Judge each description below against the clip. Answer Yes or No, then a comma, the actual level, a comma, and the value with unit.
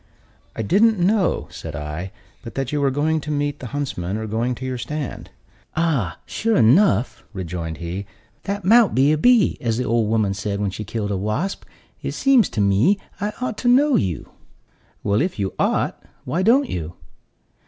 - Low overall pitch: Yes, low, 125 Hz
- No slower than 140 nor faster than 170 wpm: No, average, 185 wpm